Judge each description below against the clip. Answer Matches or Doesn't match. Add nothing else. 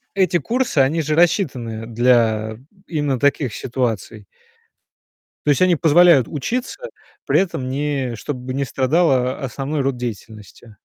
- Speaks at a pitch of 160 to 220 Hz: Doesn't match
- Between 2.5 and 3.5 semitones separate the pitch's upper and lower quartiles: Doesn't match